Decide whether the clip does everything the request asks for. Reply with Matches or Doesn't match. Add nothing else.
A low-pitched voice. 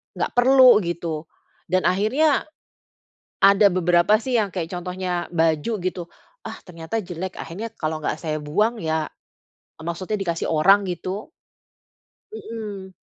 Doesn't match